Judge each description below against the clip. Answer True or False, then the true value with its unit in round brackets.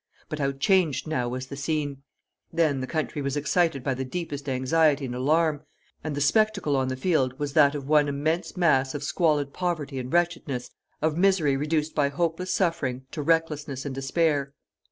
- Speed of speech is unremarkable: True (180 wpm)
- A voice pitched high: False (145 Hz)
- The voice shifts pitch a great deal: False (3.1 semitones)